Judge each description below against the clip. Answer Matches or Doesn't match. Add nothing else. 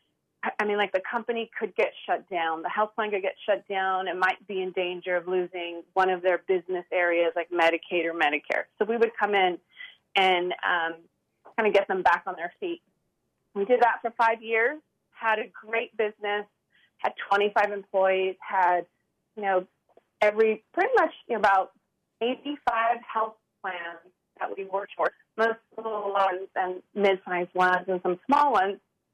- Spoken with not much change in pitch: Doesn't match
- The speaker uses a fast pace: Doesn't match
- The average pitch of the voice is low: Doesn't match